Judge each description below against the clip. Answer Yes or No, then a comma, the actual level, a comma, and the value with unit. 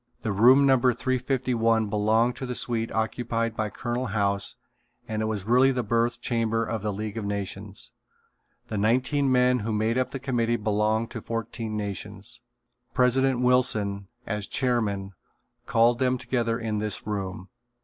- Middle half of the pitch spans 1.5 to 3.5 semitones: Yes, average, 2.8 semitones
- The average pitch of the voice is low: Yes, low, 115 Hz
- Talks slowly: No, average, 155 wpm